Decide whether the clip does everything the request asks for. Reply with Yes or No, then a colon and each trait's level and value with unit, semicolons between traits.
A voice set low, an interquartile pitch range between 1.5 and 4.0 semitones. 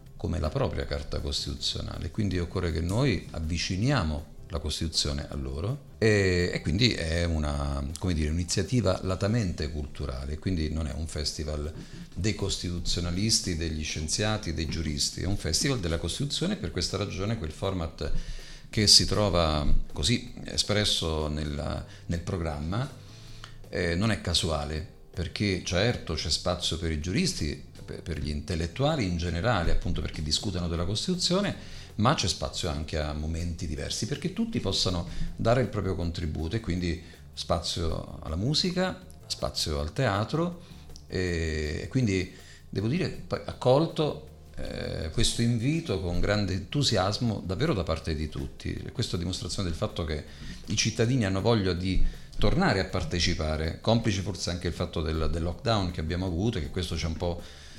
No: very low, 90 Hz; average, 4.9 semitones